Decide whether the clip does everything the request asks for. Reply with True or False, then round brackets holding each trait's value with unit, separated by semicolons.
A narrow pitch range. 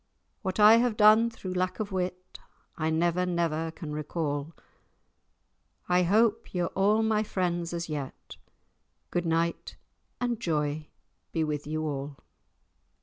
False (4.8 semitones)